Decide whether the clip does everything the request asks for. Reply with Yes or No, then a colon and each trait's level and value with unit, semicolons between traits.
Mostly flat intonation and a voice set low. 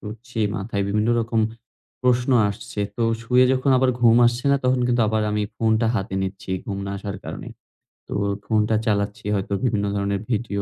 No: average, 3.0 semitones; low, 110 Hz